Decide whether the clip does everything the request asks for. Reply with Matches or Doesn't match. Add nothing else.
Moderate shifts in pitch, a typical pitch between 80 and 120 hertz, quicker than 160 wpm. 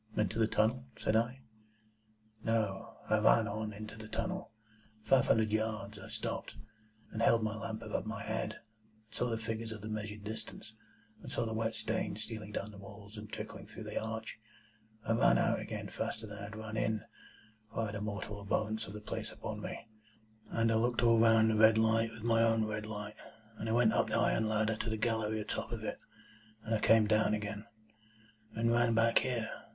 Doesn't match